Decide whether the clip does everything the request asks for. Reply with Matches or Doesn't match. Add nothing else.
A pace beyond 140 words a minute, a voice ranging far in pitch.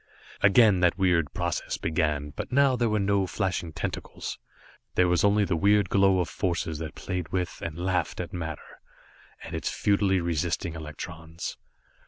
Doesn't match